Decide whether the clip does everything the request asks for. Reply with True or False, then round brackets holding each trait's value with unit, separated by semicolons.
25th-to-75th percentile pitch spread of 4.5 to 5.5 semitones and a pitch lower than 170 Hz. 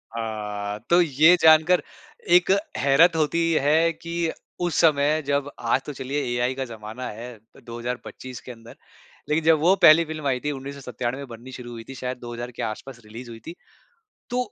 True (4.8 semitones; 135 Hz)